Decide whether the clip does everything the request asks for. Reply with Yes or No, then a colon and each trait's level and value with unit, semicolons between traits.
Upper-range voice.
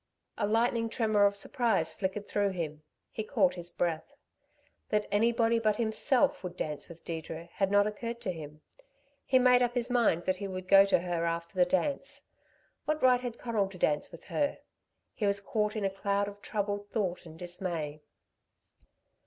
Yes: high, 200 Hz